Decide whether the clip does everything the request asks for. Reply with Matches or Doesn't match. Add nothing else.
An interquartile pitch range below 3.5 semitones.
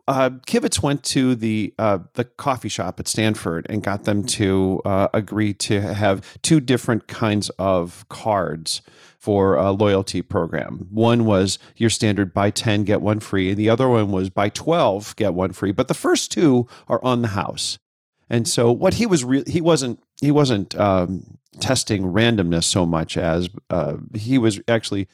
Doesn't match